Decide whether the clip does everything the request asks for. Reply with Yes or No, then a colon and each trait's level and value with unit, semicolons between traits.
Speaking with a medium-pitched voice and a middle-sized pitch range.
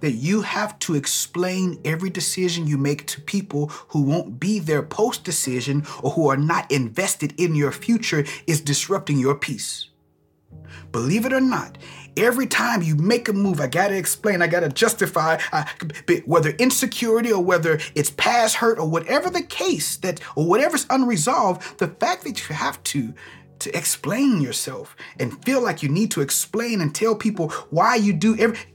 No: medium, 175 Hz; wide, 7.0 semitones